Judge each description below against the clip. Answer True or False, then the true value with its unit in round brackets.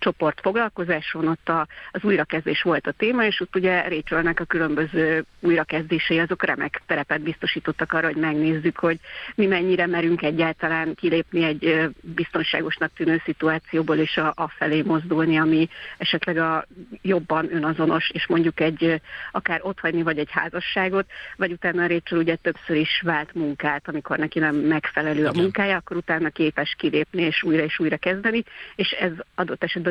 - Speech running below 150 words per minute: False (155 wpm)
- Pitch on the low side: False (165 Hz)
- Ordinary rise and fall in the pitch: False (1.7 semitones)